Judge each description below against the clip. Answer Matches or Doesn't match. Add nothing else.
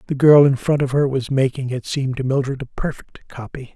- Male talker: Matches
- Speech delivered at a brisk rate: Matches